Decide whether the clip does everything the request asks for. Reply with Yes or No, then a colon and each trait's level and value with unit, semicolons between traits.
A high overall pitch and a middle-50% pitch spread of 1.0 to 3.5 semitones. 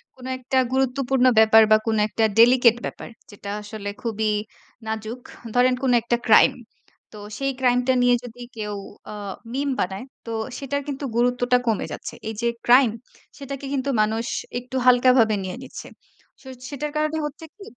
Yes: high, 245 Hz; average, 3.1 semitones